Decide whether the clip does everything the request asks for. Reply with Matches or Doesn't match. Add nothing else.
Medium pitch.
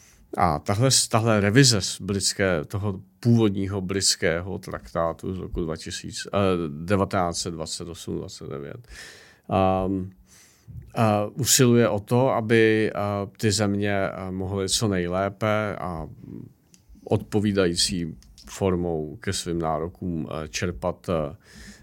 Doesn't match